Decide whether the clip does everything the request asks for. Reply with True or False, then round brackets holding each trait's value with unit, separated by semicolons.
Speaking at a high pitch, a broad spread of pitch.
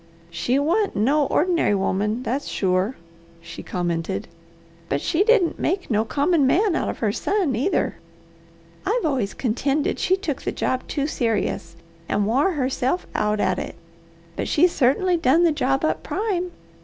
True (275 Hz; 8.4 semitones)